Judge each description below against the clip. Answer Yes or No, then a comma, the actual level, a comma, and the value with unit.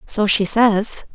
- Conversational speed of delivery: Yes, average, 155 wpm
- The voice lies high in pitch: Yes, high, 210 Hz